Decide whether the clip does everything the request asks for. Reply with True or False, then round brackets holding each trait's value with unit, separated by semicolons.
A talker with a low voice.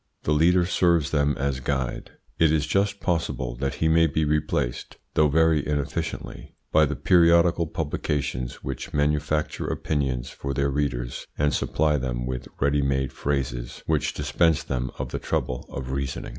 True (75 Hz)